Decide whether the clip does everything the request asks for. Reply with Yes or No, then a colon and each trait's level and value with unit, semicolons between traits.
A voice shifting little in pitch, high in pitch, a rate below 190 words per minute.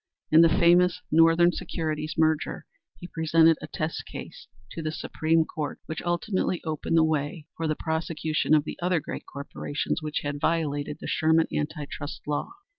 No: narrow, 1.4 semitones; medium, 160 Hz; average, 170 wpm